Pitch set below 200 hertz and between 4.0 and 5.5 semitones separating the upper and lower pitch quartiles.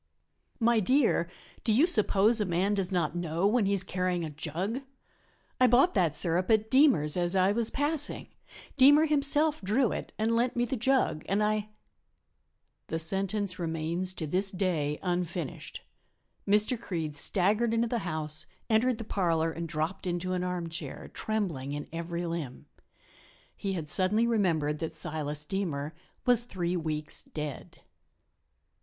Yes: medium, 185 Hz; average, 5.2 semitones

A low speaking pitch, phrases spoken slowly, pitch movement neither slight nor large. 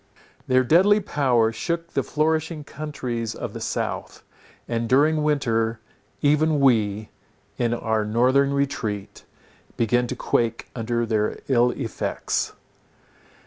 Yes: low, 125 Hz; slow, 115 wpm; average, 4.6 semitones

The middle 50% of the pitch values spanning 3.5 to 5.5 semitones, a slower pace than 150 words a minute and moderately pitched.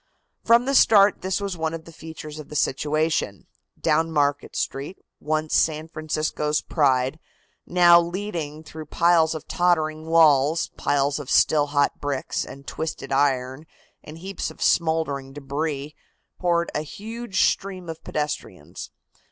No: average, 2.8 semitones; average, 140 wpm; medium, 155 Hz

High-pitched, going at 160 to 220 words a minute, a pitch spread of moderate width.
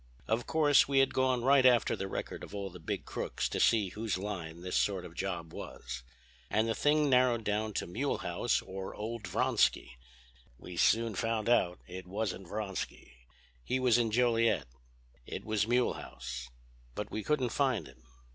No: low, 110 Hz; average, 170 wpm; average, 4.8 semitones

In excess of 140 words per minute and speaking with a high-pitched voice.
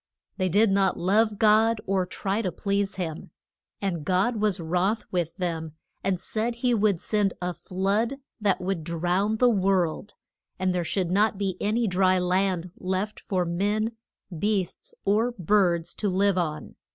Yes: average, 160 wpm; high, 195 Hz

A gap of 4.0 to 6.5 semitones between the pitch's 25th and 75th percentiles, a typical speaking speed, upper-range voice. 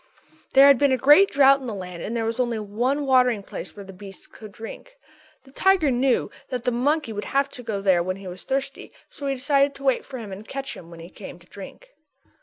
No: wide, 5.4 semitones; fast, 250 wpm; high, 245 Hz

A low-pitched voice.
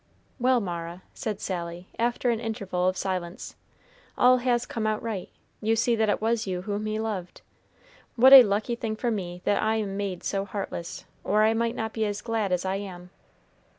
No: high, 210 Hz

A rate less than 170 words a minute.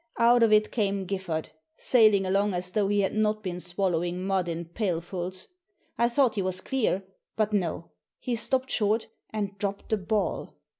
No: average, 180 wpm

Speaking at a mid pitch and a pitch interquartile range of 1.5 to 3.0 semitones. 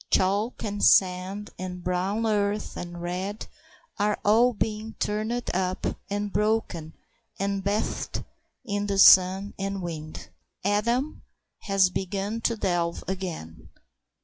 No: high, 200 Hz; narrow, 2.4 semitones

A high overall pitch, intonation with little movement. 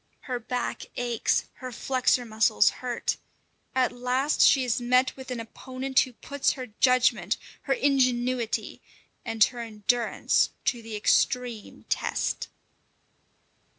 Yes: very high, 250 Hz; narrow, 1.8 semitones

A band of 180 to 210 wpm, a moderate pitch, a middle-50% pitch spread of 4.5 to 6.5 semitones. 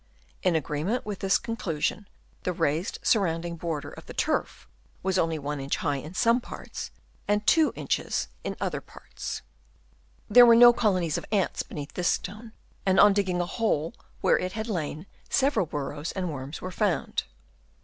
No: average, 170 wpm; medium, 180 Hz; average, 5.1 semitones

